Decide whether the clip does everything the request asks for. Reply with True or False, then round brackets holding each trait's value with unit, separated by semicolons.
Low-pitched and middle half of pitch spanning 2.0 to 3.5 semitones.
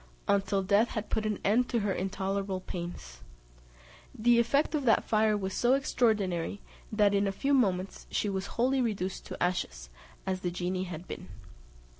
False (200 Hz; 3.1 semitones)